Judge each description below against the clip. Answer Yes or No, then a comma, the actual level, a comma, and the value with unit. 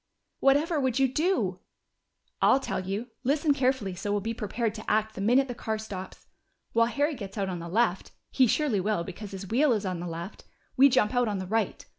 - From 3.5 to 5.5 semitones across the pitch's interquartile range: Yes, average, 5.1 semitones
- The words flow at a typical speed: No, fast, 215 wpm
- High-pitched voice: Yes, high, 220 Hz